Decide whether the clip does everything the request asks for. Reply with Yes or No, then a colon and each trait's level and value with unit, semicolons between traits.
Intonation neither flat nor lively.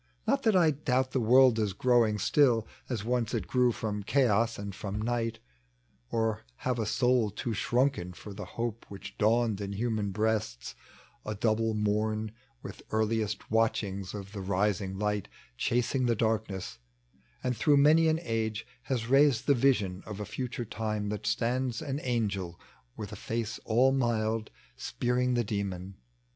Yes: average, 3.0 semitones